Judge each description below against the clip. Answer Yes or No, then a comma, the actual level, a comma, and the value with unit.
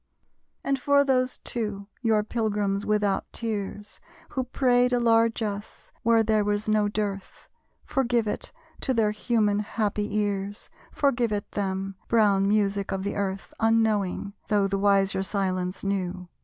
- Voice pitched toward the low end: No, high, 210 Hz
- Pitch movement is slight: Yes, narrow, 2.3 semitones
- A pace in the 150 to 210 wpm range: No, average, 140 wpm